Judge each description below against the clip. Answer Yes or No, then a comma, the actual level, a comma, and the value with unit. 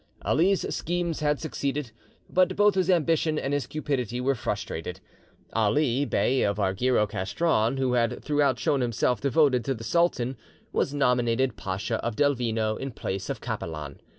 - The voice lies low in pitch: Yes, low, 130 Hz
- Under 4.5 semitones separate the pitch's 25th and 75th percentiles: No, average, 4.8 semitones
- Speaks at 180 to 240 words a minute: No, average, 150 wpm